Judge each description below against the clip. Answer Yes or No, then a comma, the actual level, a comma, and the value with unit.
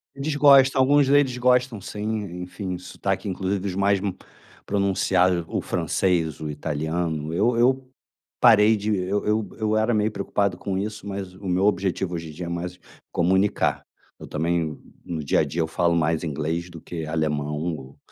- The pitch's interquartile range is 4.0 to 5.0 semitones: Yes, average, 4.3 semitones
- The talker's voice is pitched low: Yes, very low, 95 Hz